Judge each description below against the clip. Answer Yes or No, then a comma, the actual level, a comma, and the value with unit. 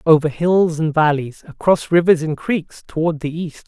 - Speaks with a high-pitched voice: No, medium, 160 Hz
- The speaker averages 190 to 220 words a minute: No, average, 180 wpm